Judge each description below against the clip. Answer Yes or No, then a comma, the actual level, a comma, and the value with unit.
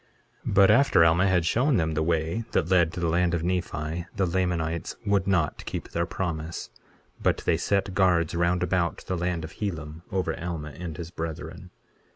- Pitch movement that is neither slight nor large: No, narrow, 2.2 semitones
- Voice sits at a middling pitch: No, very low, 85 Hz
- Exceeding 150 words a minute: Yes, average, 190 wpm